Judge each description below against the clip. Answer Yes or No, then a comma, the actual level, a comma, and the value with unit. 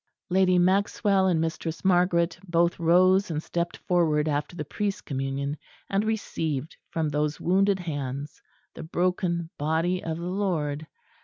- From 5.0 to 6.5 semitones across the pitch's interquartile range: No, average, 3.3 semitones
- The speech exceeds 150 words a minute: No, average, 140 wpm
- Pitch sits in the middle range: Yes, medium, 170 Hz